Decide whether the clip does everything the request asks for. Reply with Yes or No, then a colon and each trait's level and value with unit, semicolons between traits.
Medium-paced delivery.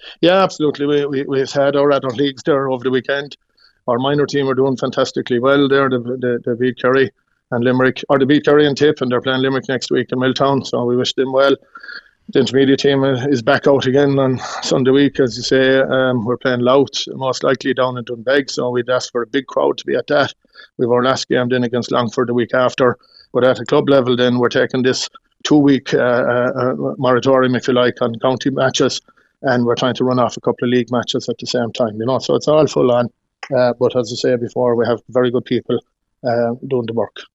No: fast, 235 wpm